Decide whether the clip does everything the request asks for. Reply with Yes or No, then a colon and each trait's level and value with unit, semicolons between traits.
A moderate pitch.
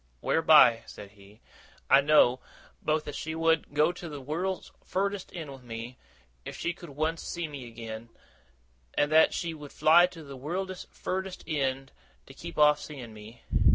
Yes: medium, 150 Hz